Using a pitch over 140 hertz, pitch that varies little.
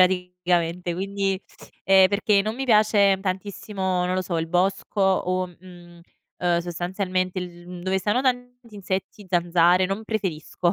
Yes: medium, 185 Hz; narrow, 2.0 semitones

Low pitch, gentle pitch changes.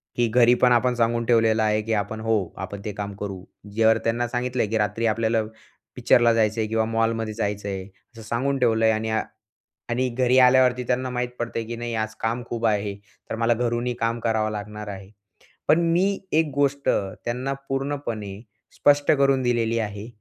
Yes: low, 115 Hz; narrow, 2.3 semitones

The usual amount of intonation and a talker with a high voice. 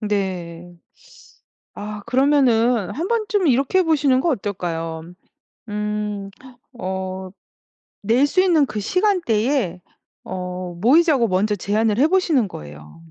No: wide, 7.3 semitones; high, 215 Hz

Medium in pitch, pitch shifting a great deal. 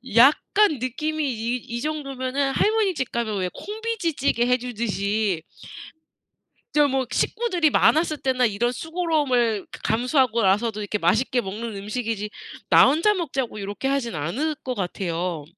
No: very high, 250 Hz; wide, 5.9 semitones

